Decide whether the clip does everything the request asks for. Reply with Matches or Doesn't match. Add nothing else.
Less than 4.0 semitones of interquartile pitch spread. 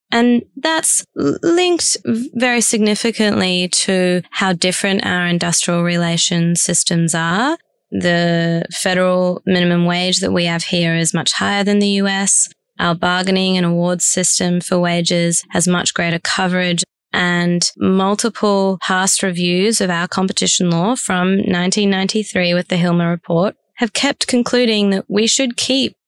Matches